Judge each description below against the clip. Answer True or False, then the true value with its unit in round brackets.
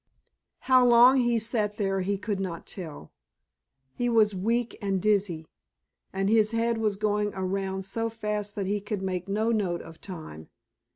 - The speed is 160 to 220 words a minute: True (165 wpm)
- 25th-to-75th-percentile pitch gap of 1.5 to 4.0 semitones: True (2.8 semitones)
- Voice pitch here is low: False (205 Hz)